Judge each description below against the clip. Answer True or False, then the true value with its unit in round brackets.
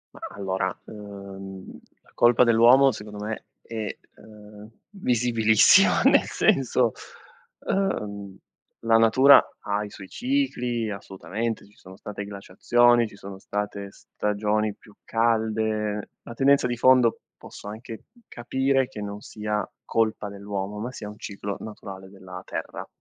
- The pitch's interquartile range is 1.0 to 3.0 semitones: True (2.6 semitones)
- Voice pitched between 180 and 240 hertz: False (105 Hz)